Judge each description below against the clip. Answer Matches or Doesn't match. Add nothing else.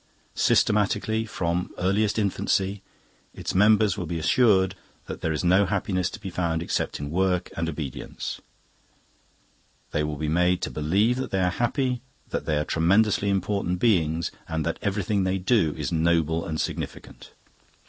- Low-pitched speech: Matches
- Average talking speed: Matches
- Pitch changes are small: Doesn't match